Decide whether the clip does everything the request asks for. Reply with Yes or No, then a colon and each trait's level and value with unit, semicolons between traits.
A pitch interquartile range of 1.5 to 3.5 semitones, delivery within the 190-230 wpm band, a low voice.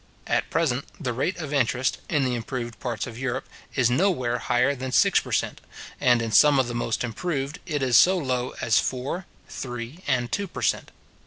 Yes: average, 2.9 semitones; average, 195 wpm; low, 130 Hz